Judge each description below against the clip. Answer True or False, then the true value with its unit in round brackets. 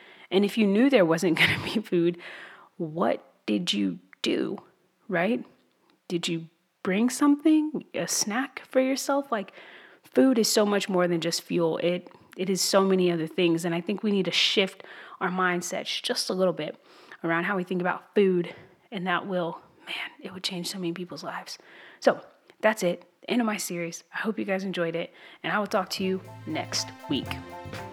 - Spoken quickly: False (195 wpm)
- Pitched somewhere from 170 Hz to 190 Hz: True (185 Hz)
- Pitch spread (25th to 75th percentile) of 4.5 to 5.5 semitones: False (3.3 semitones)